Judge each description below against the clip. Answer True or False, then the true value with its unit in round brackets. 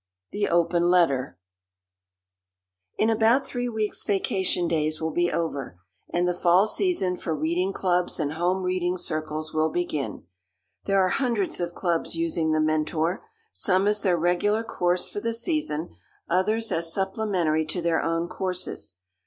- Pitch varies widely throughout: False (3.2 semitones)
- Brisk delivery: False (150 wpm)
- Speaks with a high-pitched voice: False (175 Hz)